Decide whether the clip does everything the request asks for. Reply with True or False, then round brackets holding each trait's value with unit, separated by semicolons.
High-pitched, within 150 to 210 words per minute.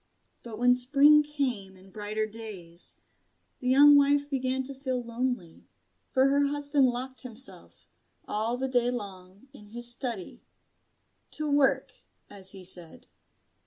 False (250 Hz; 135 wpm)